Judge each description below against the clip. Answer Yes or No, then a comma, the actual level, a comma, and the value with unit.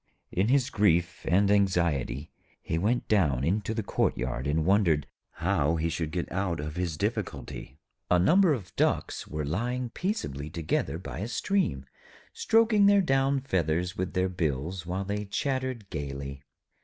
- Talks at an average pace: Yes, average, 155 wpm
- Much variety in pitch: Yes, wide, 5.8 semitones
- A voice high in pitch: No, very low, 90 Hz